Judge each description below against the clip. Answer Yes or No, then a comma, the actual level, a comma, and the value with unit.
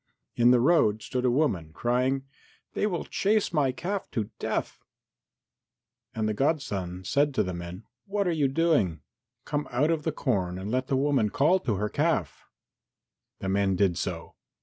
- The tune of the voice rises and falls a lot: Yes, wide, 7.1 semitones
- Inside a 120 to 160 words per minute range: No, average, 170 wpm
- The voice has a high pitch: No, low, 125 Hz